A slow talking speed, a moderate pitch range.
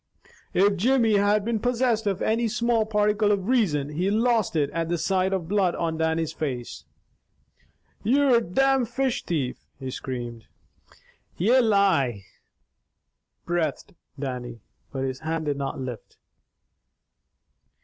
No: slow, 130 wpm; wide, 7.1 semitones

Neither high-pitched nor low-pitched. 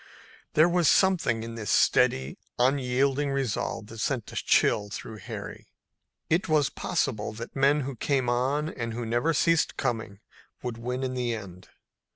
No: low, 125 Hz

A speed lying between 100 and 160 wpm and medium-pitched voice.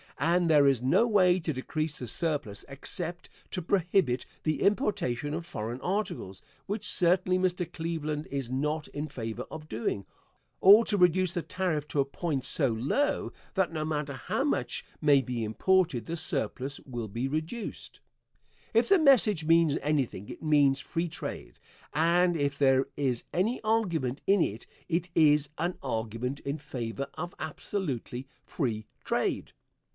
Yes: average, 155 wpm; medium, 155 Hz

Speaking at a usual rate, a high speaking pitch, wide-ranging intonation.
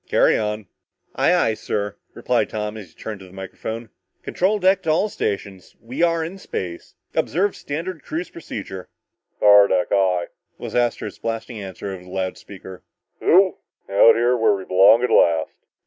No: average, 165 wpm; low, 105 Hz; wide, 8.2 semitones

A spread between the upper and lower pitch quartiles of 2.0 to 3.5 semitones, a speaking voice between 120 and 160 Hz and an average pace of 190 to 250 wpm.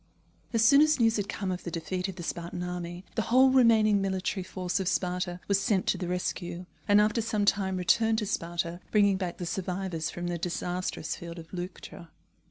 No: average, 2.9 semitones; medium, 185 Hz; average, 200 wpm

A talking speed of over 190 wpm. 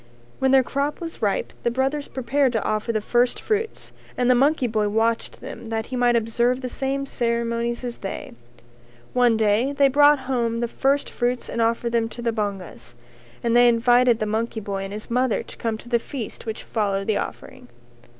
Yes: average, 200 wpm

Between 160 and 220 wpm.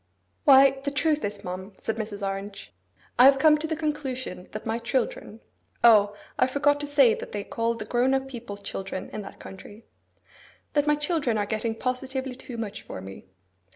Yes: average, 180 wpm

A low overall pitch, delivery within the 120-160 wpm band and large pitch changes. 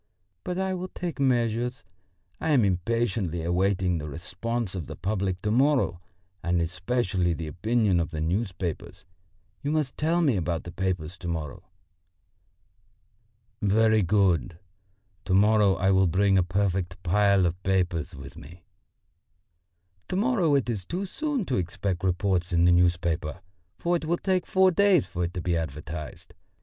Yes: very low, 95 Hz; average, 155 wpm; wide, 5.7 semitones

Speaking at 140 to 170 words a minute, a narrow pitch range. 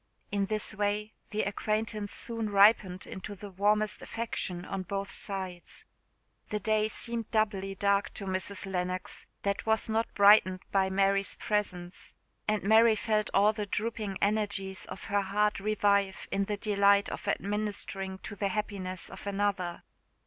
Yes: average, 150 wpm; narrow, 1.6 semitones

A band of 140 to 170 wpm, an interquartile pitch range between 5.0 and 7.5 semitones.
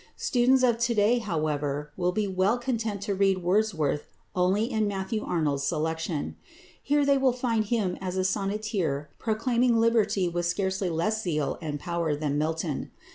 Yes: average, 160 wpm; wide, 5.4 semitones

